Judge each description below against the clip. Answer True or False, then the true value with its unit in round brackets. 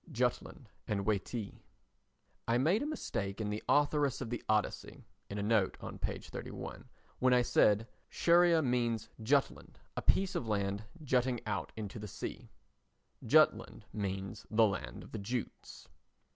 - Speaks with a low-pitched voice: True (115 Hz)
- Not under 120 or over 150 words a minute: True (145 wpm)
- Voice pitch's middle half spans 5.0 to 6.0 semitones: False (3.8 semitones)